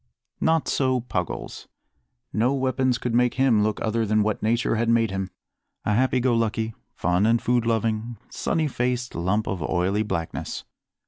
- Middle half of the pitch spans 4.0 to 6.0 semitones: No, average, 2.7 semitones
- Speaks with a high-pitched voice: No, low, 115 Hz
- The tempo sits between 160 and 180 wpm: Yes, average, 165 wpm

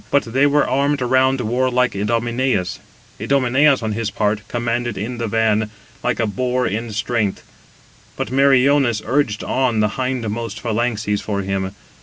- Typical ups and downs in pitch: Yes, average, 3.3 semitones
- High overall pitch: No, low, 120 Hz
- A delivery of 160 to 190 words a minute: No, average, 145 wpm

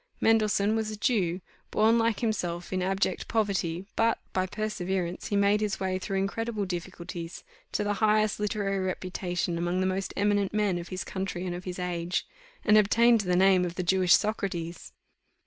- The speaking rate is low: No, average, 175 wpm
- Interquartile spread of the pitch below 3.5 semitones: Yes, average, 2.8 semitones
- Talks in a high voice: Yes, high, 195 Hz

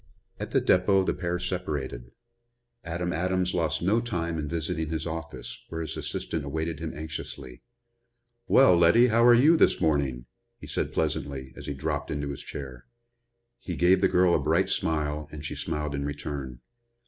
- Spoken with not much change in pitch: No, average, 3.7 semitones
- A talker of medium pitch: No, very low, 80 Hz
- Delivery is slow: No, average, 170 wpm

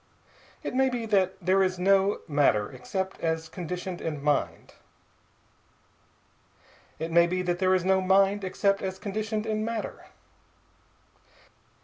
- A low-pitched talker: No, high, 190 Hz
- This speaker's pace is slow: Yes, slow, 130 wpm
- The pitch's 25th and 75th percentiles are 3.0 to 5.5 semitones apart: No, narrow, 2.5 semitones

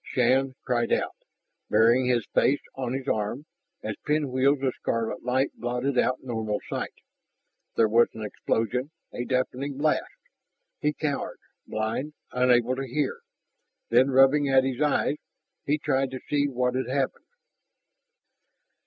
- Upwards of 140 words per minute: No, slow, 135 wpm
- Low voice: Yes, low, 130 Hz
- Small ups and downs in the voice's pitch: Yes, narrow, 2.3 semitones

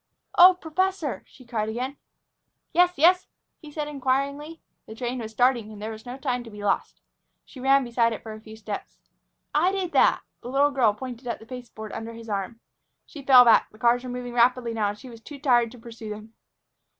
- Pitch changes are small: No, average, 3.8 semitones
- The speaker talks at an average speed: No, fast, 210 wpm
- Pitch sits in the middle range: No, high, 245 Hz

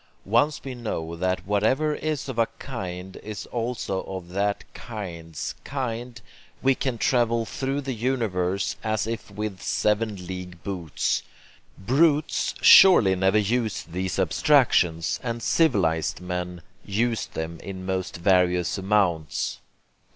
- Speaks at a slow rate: Yes, slow, 125 wpm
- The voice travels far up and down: No, average, 4.9 semitones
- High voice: No, low, 105 Hz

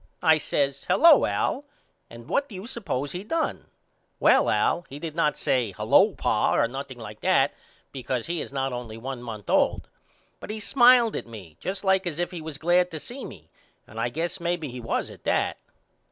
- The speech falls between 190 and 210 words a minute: Yes, average, 200 wpm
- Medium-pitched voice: Yes, medium, 155 Hz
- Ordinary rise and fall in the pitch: No, wide, 6.8 semitones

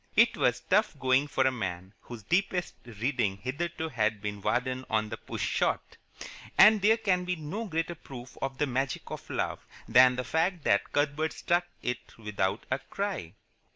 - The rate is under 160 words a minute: No, average, 175 wpm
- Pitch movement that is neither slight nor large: No, wide, 6.9 semitones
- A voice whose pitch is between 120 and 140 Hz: Yes, low, 135 Hz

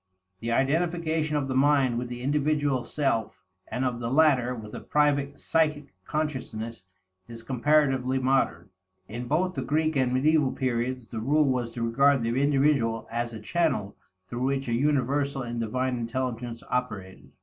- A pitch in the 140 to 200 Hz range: No, low, 130 Hz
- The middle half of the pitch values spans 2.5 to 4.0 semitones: Yes, average, 3.6 semitones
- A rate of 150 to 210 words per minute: Yes, average, 160 wpm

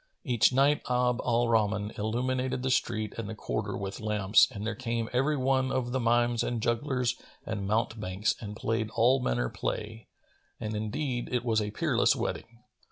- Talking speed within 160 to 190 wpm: Yes, average, 170 wpm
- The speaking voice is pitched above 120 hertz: No, low, 115 Hz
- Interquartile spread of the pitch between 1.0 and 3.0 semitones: Yes, average, 2.7 semitones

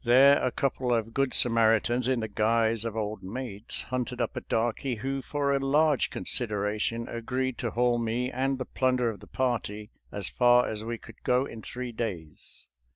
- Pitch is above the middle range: No, low, 120 Hz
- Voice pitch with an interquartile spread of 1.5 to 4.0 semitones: Yes, narrow, 2.6 semitones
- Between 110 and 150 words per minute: No, average, 185 wpm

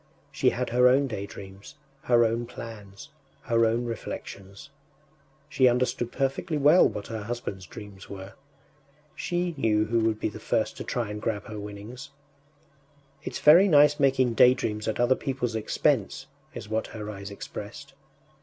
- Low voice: Yes, low, 115 Hz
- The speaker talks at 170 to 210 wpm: No, average, 155 wpm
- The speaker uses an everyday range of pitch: Yes, average, 3.9 semitones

